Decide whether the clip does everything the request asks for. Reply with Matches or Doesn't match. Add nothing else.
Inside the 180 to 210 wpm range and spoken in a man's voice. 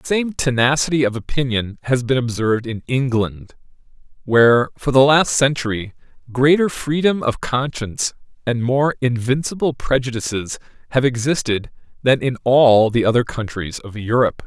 Doesn't match